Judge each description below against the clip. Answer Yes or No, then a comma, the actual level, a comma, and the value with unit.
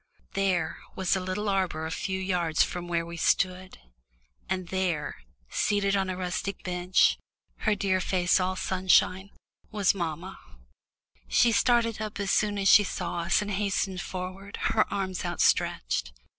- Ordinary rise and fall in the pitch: No, narrow, 1.9 semitones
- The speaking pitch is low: No, medium, 185 Hz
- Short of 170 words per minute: Yes, average, 150 wpm